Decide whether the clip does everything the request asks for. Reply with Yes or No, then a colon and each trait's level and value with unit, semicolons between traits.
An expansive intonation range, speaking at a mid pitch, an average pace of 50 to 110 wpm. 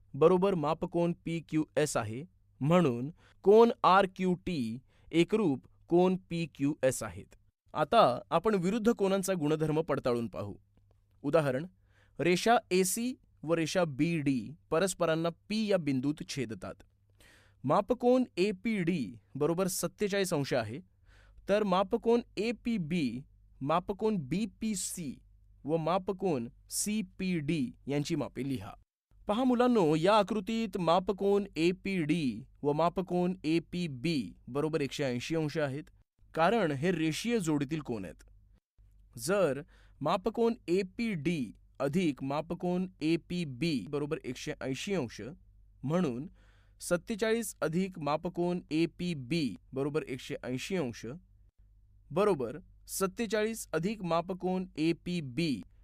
No: wide, 7.1 semitones; medium, 165 Hz; average, 125 wpm